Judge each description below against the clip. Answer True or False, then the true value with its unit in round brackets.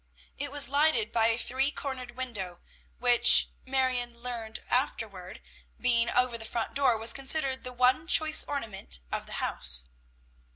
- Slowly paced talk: False (150 wpm)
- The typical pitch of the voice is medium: False (250 Hz)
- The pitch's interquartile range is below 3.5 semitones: True (2.9 semitones)